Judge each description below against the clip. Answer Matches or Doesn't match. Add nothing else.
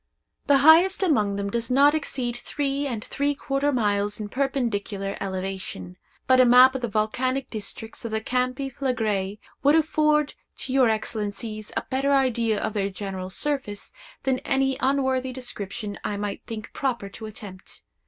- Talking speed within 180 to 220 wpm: Doesn't match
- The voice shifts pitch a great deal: Doesn't match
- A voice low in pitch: Doesn't match